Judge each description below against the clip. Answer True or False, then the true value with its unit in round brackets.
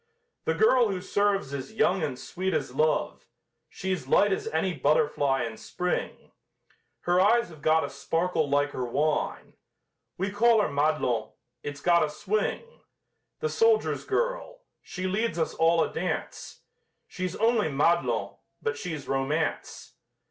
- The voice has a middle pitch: True (170 Hz)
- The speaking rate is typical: True (145 wpm)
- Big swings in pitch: True (5.8 semitones)